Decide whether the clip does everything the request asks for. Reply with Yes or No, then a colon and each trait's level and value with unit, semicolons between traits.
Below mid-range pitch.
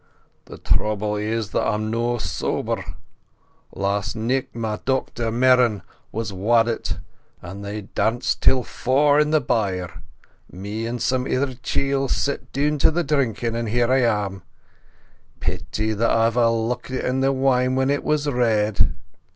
Yes: low, 115 Hz